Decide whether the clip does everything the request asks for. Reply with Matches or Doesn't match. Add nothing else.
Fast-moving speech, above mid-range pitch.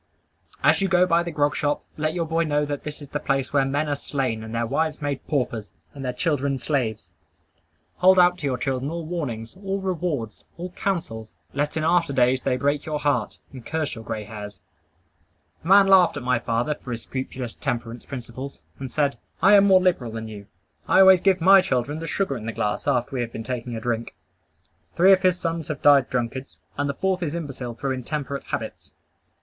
Doesn't match